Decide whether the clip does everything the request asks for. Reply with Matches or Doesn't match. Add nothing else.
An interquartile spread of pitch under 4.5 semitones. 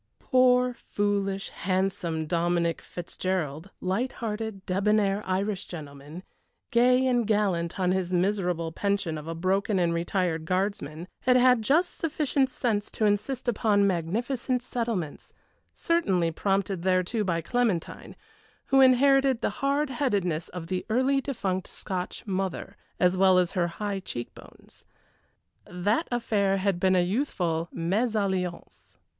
Doesn't match